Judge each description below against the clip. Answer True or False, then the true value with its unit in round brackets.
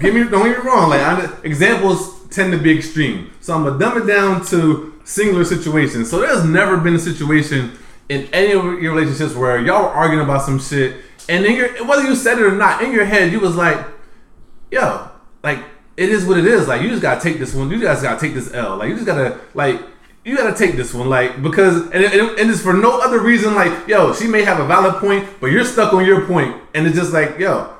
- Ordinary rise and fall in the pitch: True (4.6 semitones)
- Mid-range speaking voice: True (180 Hz)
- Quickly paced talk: True (255 wpm)